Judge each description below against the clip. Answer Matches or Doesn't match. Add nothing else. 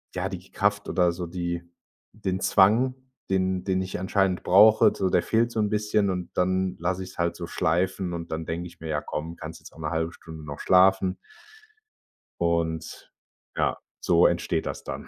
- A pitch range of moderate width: Doesn't match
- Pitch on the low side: Matches